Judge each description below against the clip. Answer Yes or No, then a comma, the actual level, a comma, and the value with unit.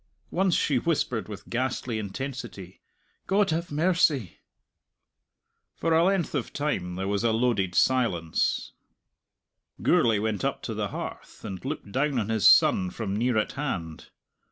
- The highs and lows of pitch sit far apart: Yes, wide, 6.8 semitones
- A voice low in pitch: Yes, low, 120 Hz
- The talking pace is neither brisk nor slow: Yes, average, 145 wpm